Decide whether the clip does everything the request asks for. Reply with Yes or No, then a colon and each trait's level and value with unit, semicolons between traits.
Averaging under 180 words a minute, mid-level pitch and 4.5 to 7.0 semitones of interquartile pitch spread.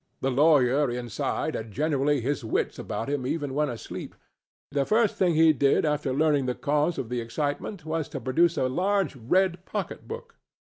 No: average, 170 wpm; medium, 145 Hz; average, 4.0 semitones